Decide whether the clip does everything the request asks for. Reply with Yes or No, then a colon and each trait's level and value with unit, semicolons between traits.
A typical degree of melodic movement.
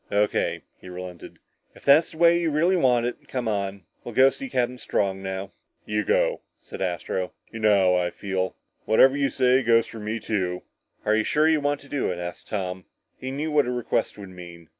No: wide, 6.1 semitones